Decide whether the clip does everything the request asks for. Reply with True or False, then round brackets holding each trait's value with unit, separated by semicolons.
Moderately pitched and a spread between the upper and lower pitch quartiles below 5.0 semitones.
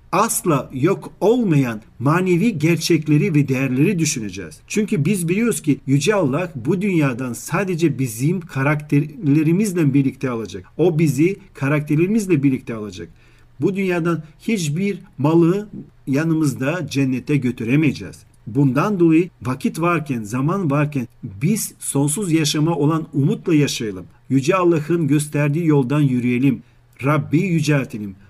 True (150 Hz; 4.2 semitones)